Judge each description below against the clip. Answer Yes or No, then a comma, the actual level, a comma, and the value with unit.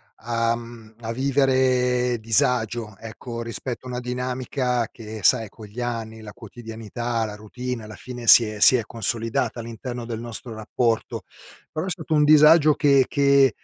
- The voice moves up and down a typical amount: No, narrow, 2.2 semitones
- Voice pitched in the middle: No, low, 120 Hz